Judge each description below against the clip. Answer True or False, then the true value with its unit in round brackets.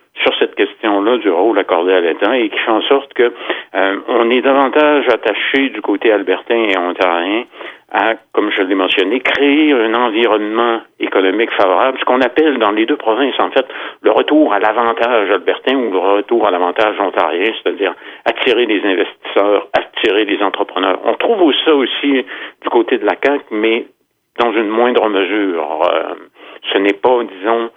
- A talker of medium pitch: False (115 Hz)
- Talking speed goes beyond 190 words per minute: False (175 wpm)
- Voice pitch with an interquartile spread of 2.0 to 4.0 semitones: False (4.7 semitones)